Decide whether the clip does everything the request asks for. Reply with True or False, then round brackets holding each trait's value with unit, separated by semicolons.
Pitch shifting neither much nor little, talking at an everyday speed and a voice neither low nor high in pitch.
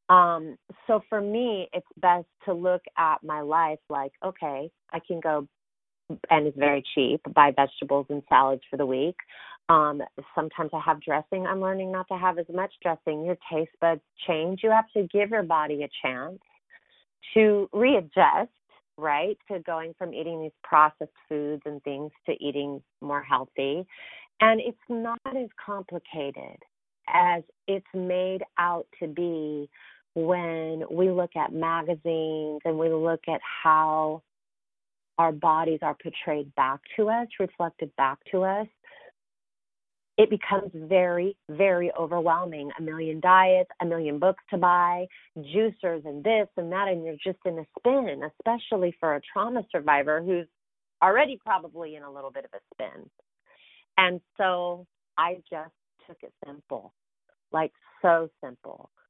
True (3.5 semitones; 150 wpm; 170 Hz)